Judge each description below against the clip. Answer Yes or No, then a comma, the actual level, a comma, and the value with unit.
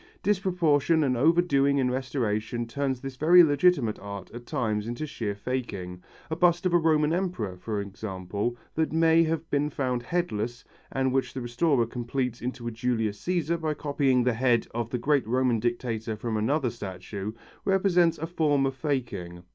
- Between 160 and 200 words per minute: Yes, average, 170 wpm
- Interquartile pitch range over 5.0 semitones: Yes, wide, 5.4 semitones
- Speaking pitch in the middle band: No, low, 130 Hz